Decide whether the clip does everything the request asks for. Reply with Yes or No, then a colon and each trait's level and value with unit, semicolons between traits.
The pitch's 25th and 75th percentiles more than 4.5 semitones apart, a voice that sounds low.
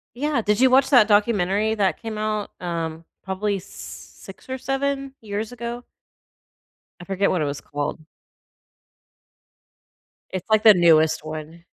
No: wide, 5.4 semitones; high, 210 Hz